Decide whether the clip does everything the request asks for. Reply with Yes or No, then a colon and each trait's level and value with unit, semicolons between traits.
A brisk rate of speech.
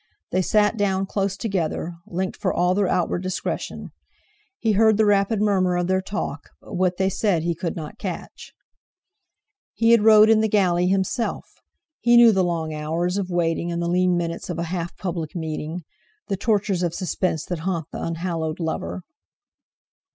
No: average, 175 wpm